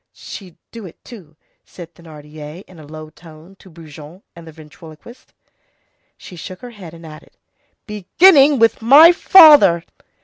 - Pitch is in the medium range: Yes, medium, 170 Hz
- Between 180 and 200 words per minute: No, average, 145 wpm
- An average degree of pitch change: No, wide, 6.4 semitones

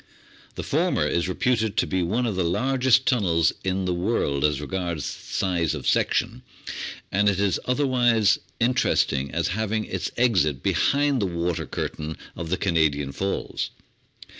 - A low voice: Yes, very low, 95 Hz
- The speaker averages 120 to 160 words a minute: Yes, average, 150 wpm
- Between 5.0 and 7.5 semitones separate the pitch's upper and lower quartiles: Yes, wide, 5.6 semitones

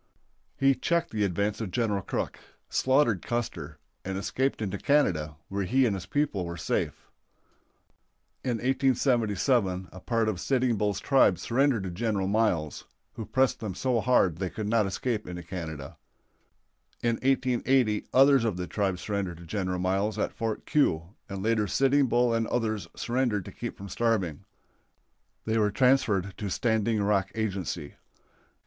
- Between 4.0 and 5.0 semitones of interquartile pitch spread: Yes, average, 4.4 semitones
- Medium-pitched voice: No, low, 105 Hz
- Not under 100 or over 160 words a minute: Yes, average, 155 wpm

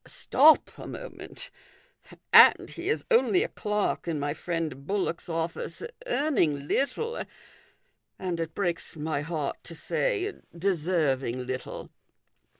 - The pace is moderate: No, slow, 120 wpm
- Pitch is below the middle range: No, medium, 170 Hz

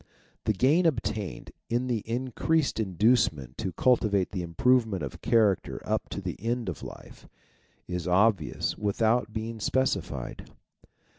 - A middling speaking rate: No, slow, 130 wpm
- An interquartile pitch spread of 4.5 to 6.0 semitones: Yes, average, 4.8 semitones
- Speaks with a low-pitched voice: Yes, low, 110 Hz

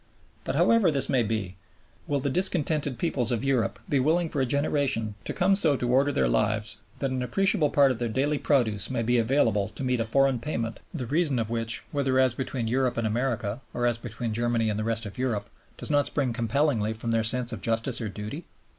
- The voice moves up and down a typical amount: Yes, average, 3.8 semitones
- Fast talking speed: Yes, fast, 220 wpm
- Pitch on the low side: Yes, low, 125 Hz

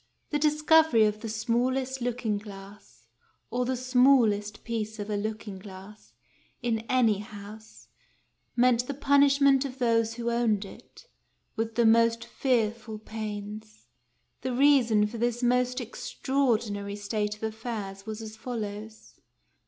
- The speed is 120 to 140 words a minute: Yes, slow, 135 wpm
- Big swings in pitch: No, average, 3.0 semitones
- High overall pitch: Yes, high, 225 Hz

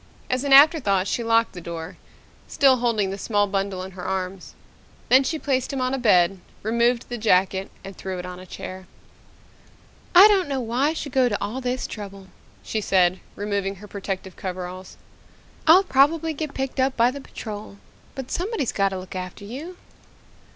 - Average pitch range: No, wide, 5.7 semitones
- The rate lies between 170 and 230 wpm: Yes, average, 185 wpm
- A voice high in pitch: Yes, high, 215 Hz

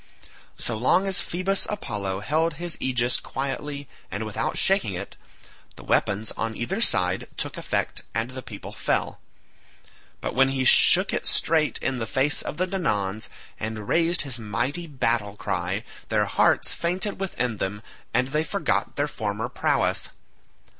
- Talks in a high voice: No, low, 130 Hz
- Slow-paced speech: No, average, 155 wpm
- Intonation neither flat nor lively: No, wide, 7.7 semitones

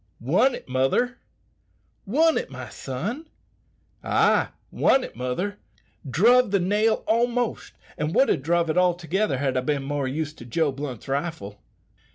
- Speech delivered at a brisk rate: No, average, 150 wpm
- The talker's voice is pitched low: No, medium, 165 Hz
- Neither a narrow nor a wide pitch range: No, wide, 8.4 semitones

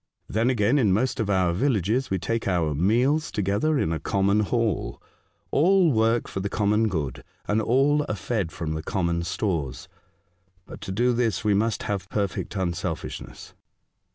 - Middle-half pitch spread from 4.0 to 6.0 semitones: Yes, average, 4.3 semitones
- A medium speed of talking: Yes, average, 170 wpm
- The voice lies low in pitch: Yes, low, 105 Hz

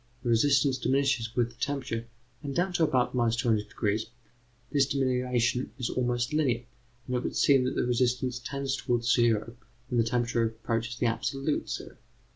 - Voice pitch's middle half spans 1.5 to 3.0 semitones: Yes, narrow, 2.5 semitones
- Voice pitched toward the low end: Yes, low, 125 Hz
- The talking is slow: No, average, 160 wpm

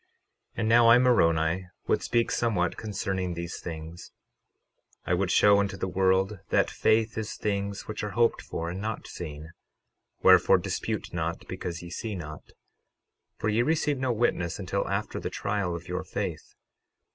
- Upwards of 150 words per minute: Yes, average, 165 wpm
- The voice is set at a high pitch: No, very low, 95 Hz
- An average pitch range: Yes, average, 4.2 semitones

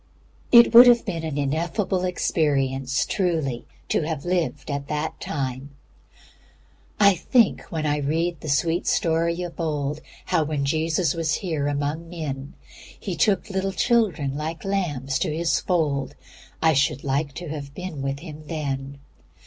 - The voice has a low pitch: No, medium, 155 Hz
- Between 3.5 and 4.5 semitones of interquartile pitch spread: Yes, average, 3.8 semitones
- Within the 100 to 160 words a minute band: Yes, average, 150 wpm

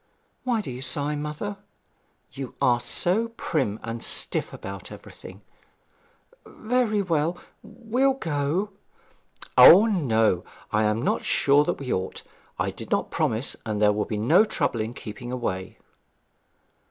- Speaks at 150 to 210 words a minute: No, average, 140 wpm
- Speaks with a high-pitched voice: No, medium, 140 Hz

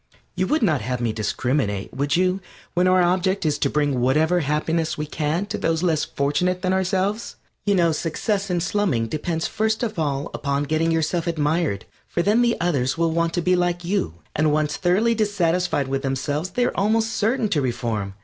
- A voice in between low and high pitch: Yes, medium, 165 Hz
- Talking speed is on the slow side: No, average, 195 wpm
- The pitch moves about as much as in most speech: Yes, average, 4.3 semitones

